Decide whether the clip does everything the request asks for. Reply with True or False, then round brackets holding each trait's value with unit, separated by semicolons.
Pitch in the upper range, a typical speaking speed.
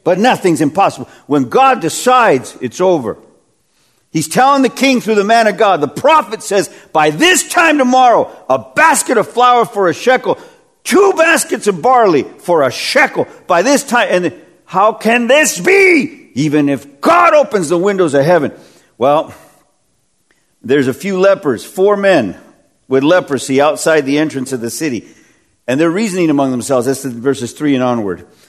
True (210 Hz; 170 wpm)